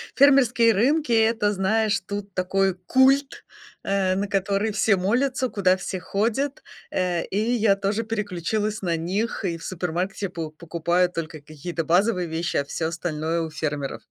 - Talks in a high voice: Yes, high, 195 Hz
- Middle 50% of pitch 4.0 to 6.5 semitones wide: Yes, average, 4.3 semitones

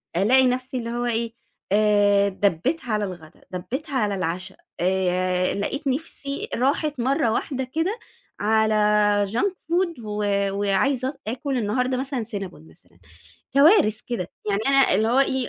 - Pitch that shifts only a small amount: No, average, 5.1 semitones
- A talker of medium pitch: No, high, 235 Hz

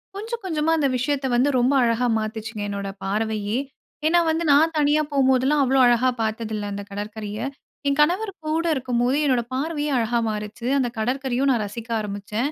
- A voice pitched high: Yes, very high, 250 Hz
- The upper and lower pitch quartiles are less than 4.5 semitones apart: No, average, 5.0 semitones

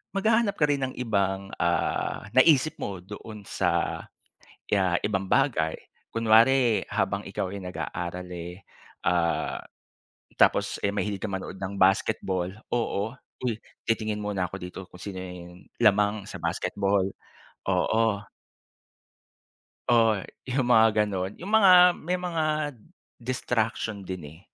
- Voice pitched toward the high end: No, low, 105 Hz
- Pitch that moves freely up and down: No, average, 4.0 semitones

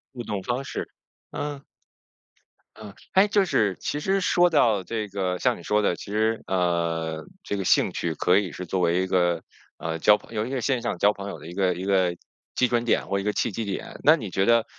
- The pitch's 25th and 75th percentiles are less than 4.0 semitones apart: No, average, 4.5 semitones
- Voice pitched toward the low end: Yes, low, 100 Hz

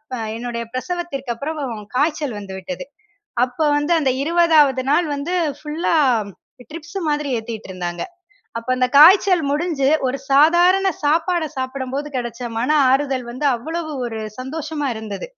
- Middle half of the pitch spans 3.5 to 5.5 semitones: Yes, average, 4.1 semitones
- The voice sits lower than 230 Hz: No, very high, 285 Hz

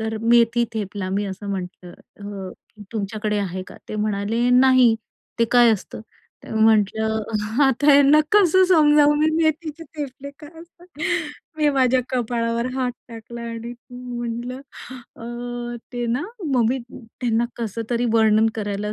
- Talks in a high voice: Yes, high, 235 Hz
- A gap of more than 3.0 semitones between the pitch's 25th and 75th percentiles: Yes, average, 3.6 semitones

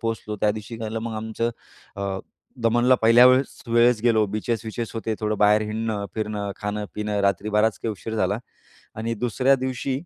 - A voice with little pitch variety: Yes, narrow, 1.7 semitones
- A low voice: Yes, low, 110 Hz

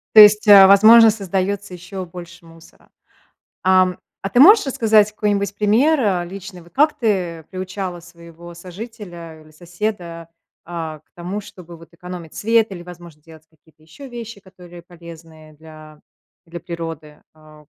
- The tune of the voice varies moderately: Yes, average, 3.6 semitones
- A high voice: No, medium, 180 Hz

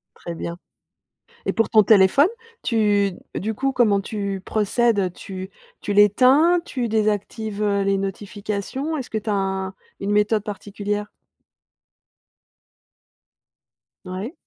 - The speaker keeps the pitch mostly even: Yes, narrow, 2.1 semitones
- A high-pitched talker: Yes, high, 205 Hz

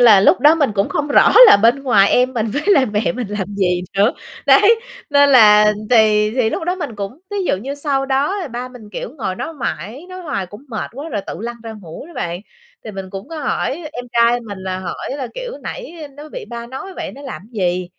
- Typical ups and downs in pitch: No, wide, 5.8 semitones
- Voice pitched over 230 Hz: Yes, high, 240 Hz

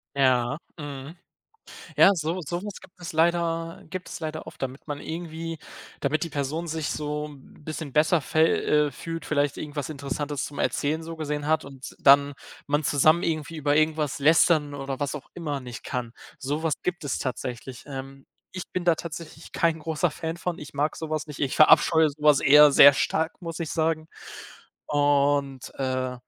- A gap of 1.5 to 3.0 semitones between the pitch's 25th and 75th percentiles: Yes, narrow, 2.5 semitones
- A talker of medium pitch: Yes, medium, 150 Hz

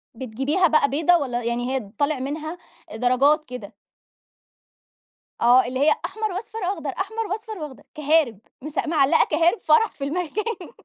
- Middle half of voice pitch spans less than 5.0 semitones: No, wide, 5.5 semitones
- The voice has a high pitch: Yes, very high, 305 Hz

